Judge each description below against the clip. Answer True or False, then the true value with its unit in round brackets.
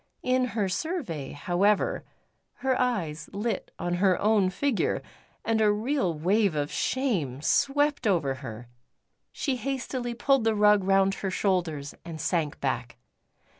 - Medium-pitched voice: False (200 Hz)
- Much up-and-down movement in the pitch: True (6.9 semitones)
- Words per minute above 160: False (135 wpm)